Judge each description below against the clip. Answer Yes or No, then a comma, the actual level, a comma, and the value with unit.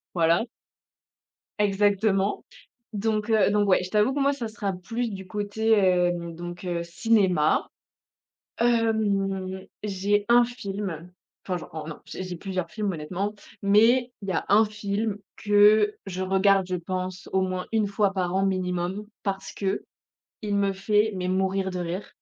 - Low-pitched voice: No, high, 195 Hz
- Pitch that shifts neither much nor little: No, narrow, 2.3 semitones